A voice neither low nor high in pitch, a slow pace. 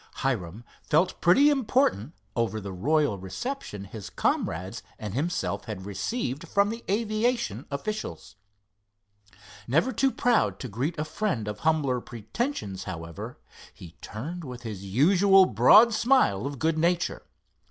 Yes: medium, 145 Hz; slow, 130 wpm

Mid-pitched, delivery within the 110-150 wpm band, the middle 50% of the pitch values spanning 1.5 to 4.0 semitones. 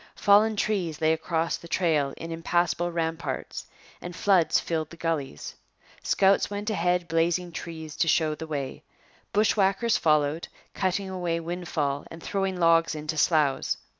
Yes: medium, 170 Hz; average, 140 wpm; narrow, 2.5 semitones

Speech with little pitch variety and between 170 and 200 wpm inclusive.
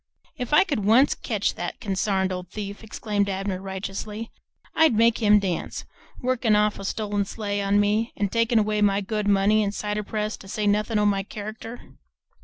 Yes: narrow, 1.7 semitones; average, 185 wpm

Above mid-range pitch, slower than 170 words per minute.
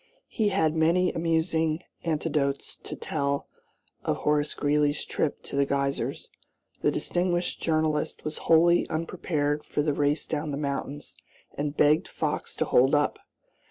No: medium, 150 Hz; average, 140 wpm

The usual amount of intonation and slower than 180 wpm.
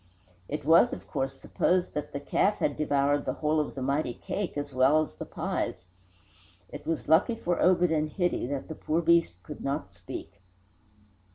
No: average, 3.4 semitones; average, 185 wpm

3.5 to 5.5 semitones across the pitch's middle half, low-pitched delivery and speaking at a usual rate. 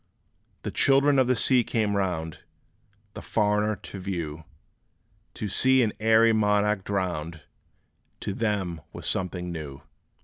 No: average, 4.0 semitones; low, 100 Hz; slow, 130 wpm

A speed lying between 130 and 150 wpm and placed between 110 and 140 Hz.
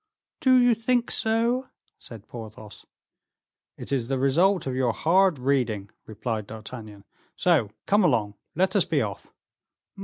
Yes: average, 140 wpm; low, 135 Hz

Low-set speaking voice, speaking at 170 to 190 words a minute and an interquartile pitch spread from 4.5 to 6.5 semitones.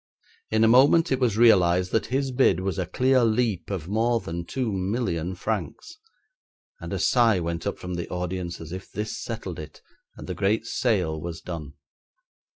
Yes: low, 100 Hz; average, 180 wpm; average, 5.1 semitones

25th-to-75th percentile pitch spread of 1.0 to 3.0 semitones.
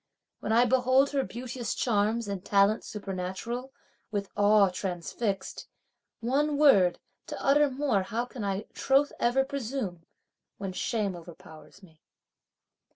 No: average, 5.1 semitones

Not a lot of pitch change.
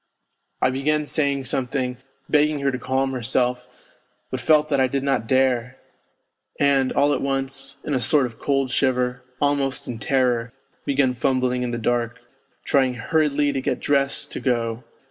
Yes: narrow, 1.9 semitones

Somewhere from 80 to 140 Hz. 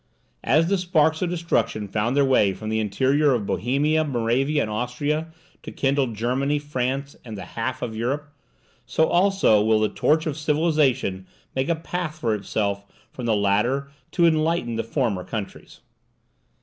Yes: low, 135 Hz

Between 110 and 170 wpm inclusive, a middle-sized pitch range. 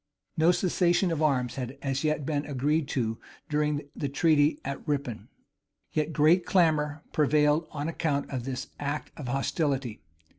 No: average, 150 wpm; narrow, 2.3 semitones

